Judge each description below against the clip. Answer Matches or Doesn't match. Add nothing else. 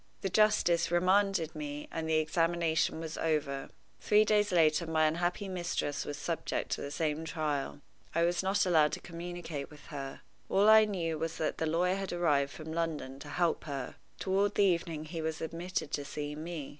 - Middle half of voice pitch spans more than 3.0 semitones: Doesn't match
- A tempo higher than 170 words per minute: Matches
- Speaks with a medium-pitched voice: Matches